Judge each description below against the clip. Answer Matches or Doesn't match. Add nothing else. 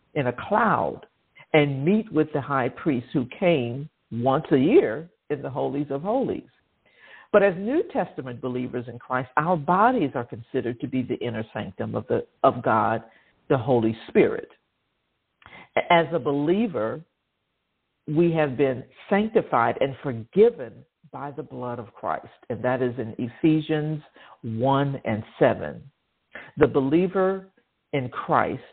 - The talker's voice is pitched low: Doesn't match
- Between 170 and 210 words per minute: Doesn't match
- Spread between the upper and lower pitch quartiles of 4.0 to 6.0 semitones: Matches